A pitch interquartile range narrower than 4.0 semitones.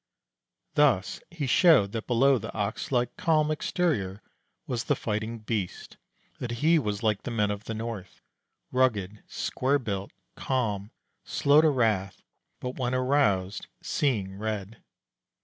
No: average, 4.5 semitones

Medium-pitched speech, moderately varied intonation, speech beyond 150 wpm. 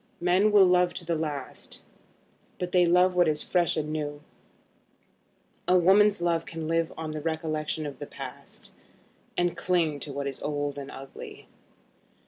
Yes: medium, 165 Hz; average, 3.1 semitones; average, 160 wpm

